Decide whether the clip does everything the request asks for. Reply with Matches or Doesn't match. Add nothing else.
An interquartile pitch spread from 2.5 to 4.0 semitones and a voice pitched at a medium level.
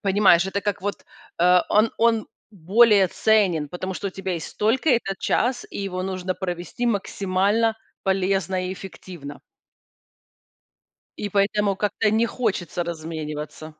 Doesn't match